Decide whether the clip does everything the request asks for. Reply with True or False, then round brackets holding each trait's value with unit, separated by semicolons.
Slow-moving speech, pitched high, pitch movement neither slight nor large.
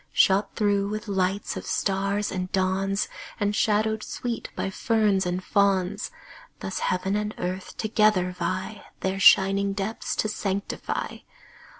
False (130 wpm; 200 Hz; 1.7 semitones)